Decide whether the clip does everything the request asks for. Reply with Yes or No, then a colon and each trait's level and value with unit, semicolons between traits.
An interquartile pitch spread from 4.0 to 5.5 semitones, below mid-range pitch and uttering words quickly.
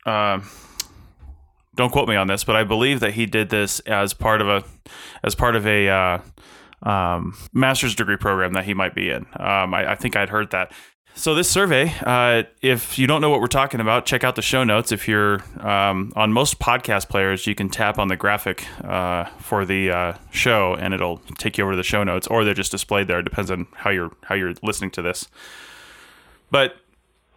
No: average, 3.1 semitones; low, 100 Hz; fast, 215 wpm